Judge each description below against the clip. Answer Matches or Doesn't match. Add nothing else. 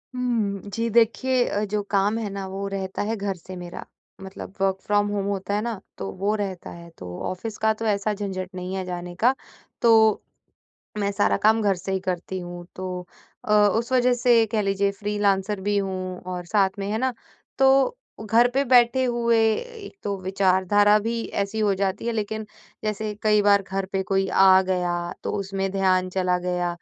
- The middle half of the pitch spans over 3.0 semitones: Doesn't match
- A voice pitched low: Doesn't match